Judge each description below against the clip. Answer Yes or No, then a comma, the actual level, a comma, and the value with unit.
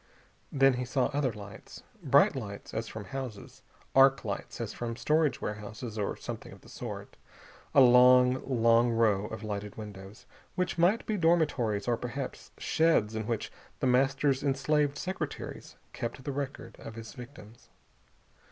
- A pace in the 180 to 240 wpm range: No, average, 150 wpm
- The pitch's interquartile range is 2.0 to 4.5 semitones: Yes, average, 4.1 semitones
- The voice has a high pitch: No, low, 125 Hz